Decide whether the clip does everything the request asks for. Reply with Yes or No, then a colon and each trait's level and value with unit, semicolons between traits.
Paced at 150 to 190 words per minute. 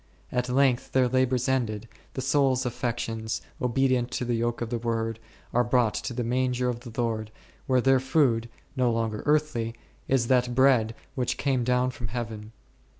Yes: average, 170 wpm